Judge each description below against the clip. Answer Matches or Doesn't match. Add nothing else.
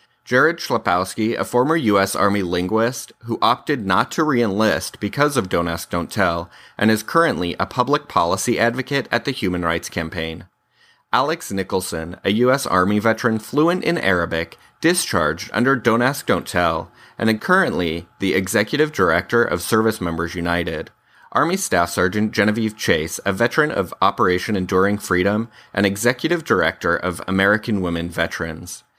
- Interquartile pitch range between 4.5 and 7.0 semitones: Matches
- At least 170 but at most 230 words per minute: Doesn't match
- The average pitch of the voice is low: Matches